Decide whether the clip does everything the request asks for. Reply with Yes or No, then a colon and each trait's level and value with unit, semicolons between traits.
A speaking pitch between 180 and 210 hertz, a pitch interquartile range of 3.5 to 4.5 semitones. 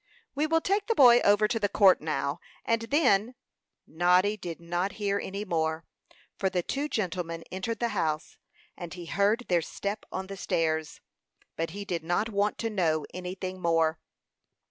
Yes: high, 190 Hz; average, 4.2 semitones